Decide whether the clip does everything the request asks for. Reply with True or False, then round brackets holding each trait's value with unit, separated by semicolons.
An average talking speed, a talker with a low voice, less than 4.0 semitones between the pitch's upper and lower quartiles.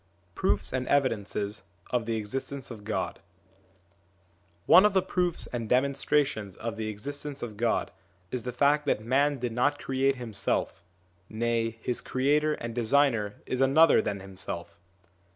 False (150 wpm; 125 Hz; 4.3 semitones)